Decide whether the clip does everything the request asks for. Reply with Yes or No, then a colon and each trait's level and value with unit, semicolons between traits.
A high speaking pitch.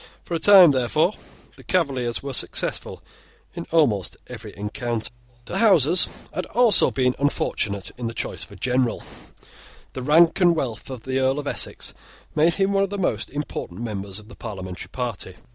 No: low, 130 Hz